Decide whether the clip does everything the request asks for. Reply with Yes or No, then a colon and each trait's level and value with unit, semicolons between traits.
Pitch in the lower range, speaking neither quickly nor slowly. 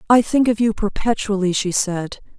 No: high, 210 Hz; average, 175 wpm